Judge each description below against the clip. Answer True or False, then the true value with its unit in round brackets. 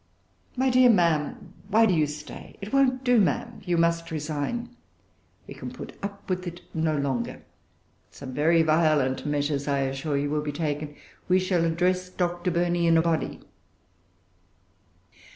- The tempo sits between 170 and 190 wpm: False (155 wpm)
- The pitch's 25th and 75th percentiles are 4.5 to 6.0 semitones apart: False (3.7 semitones)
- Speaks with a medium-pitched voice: True (165 Hz)